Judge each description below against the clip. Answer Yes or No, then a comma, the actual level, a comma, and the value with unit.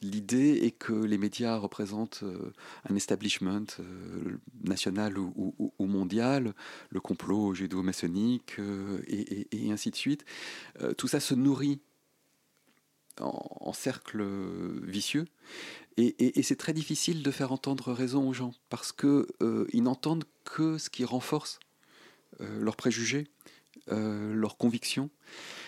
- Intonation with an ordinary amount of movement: No, wide, 5.7 semitones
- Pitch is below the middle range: Yes, low, 115 Hz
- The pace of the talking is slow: Yes, slow, 130 wpm